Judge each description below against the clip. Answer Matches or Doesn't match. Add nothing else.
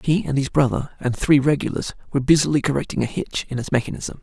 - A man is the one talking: Matches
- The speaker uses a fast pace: Matches